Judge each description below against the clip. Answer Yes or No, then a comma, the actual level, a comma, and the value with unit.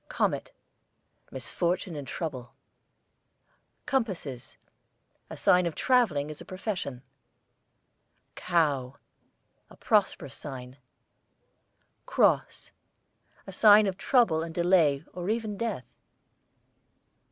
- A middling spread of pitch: No, wide, 6.3 semitones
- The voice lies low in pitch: No, medium, 170 Hz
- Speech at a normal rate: No, slow, 90 wpm